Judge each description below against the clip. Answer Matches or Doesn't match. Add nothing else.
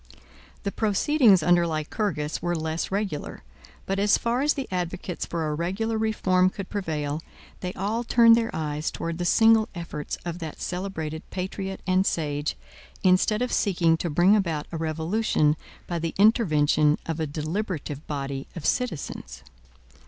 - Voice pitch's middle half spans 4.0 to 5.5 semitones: Matches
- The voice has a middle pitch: Matches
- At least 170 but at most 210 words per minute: Doesn't match